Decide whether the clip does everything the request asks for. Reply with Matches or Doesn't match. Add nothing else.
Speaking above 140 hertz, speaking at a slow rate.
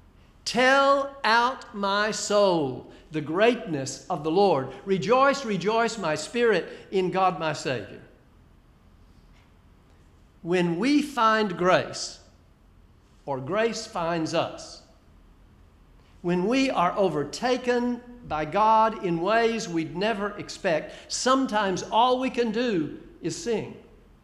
Matches